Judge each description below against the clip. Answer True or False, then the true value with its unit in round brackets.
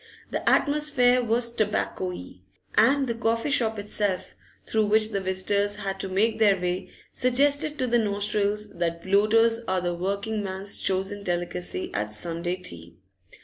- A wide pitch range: False (3.6 semitones)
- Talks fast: False (145 wpm)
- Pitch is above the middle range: True (205 Hz)